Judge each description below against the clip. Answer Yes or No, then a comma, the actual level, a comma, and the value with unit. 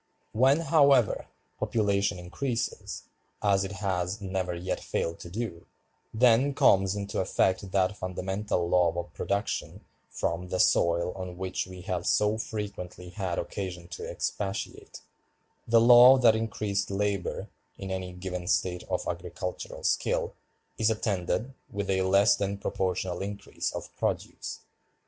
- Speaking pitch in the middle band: No, very low, 95 Hz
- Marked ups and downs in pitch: No, average, 2.7 semitones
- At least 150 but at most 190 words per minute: No, slow, 135 wpm